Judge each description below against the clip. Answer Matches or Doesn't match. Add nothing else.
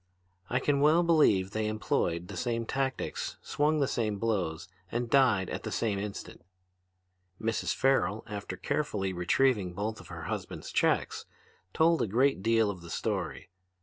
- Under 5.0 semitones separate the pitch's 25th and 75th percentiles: Doesn't match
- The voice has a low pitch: Matches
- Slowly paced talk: Doesn't match